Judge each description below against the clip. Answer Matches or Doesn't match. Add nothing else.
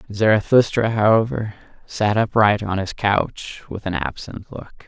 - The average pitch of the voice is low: Matches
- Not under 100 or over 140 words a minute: Matches